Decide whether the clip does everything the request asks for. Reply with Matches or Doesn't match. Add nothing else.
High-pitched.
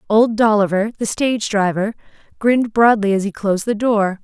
Matches